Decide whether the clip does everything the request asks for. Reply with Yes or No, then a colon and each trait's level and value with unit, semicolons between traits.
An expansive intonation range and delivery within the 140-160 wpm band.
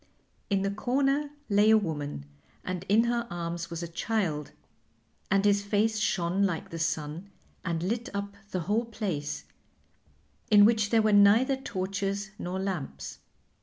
No: average, 4.1 semitones; average, 150 wpm